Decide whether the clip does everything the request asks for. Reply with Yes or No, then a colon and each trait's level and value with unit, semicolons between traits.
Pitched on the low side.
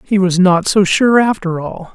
No: high, 190 Hz